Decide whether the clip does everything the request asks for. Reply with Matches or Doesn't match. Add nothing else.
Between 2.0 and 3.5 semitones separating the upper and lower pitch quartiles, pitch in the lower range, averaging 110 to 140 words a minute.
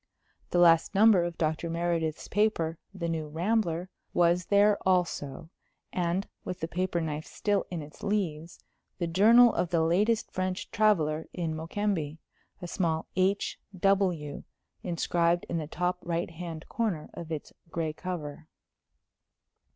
Doesn't match